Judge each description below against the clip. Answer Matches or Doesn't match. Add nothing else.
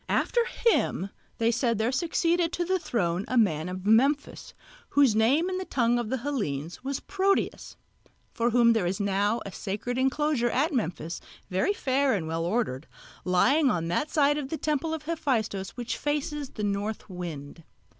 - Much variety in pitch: Matches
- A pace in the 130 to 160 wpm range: Doesn't match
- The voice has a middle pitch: Doesn't match